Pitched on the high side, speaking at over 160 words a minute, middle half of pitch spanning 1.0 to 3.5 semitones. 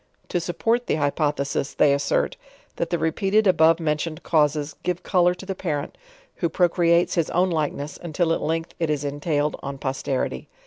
No: medium, 160 Hz; average, 170 wpm; average, 3.1 semitones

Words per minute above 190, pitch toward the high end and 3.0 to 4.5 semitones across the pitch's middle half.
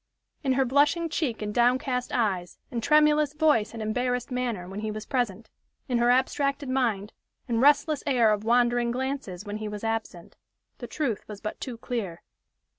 No: average, 175 wpm; high, 240 Hz; average, 3.8 semitones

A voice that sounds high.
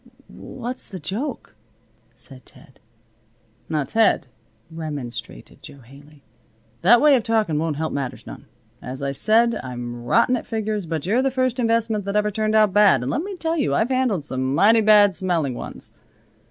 Yes: high, 200 Hz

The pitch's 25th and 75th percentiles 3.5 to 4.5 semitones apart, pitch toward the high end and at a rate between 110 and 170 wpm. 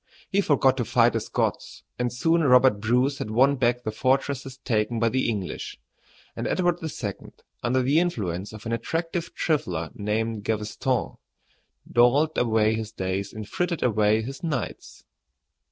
No: average, 4.2 semitones; low, 120 Hz; average, 155 wpm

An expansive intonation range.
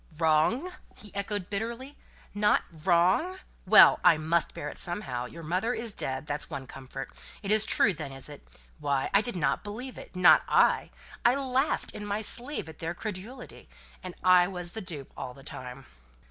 Yes: wide, 6.1 semitones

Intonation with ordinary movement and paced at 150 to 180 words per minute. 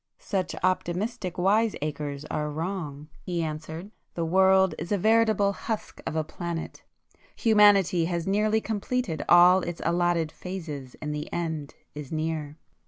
No: average, 4.0 semitones; slow, 135 wpm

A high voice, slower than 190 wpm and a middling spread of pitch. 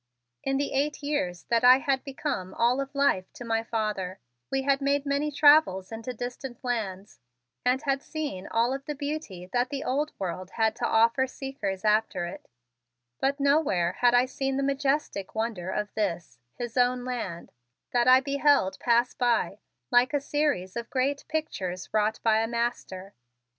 Yes: high, 245 Hz; average, 170 wpm; average, 4.7 semitones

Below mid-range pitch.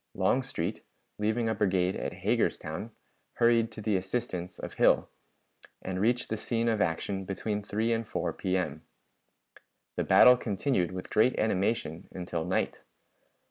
Yes: low, 105 Hz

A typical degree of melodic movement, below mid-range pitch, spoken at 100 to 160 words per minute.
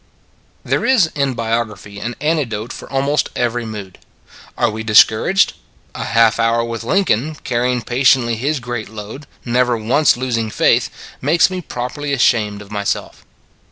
Yes: average, 3.8 semitones; low, 120 Hz; average, 150 wpm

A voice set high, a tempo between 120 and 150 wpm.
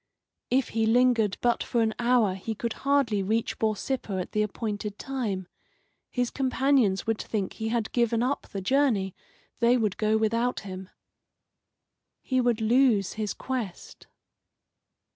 Yes: high, 225 Hz; average, 145 wpm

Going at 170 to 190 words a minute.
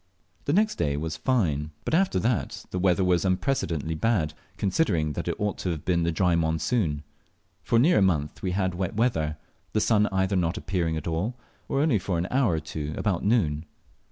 No: average, 200 wpm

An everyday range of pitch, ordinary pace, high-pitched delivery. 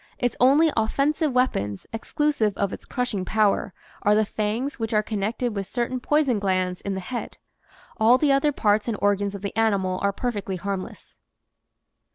Yes: average, 3.9 semitones; average, 170 wpm; high, 215 Hz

